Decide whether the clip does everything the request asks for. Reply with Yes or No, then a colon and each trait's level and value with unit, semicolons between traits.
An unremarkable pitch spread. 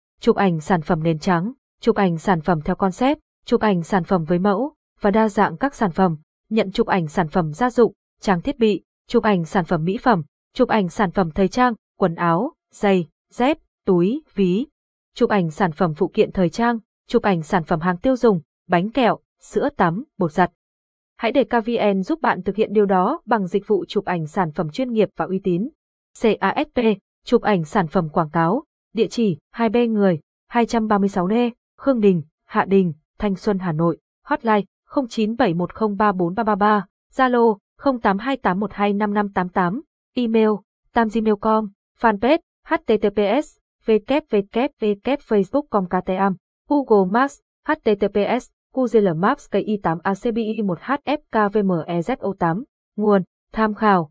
Yes: average, 3.8 semitones